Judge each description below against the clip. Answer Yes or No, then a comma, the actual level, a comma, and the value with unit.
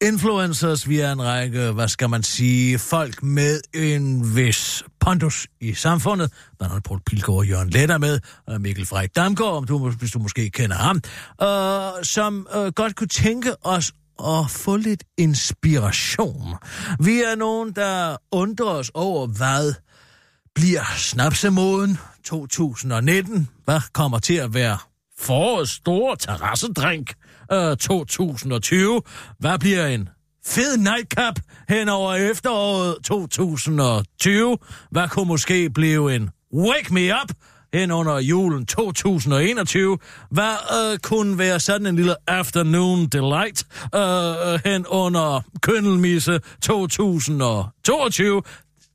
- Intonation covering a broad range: Yes, wide, 7.1 semitones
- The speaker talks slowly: Yes, slow, 125 wpm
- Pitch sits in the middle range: Yes, medium, 165 Hz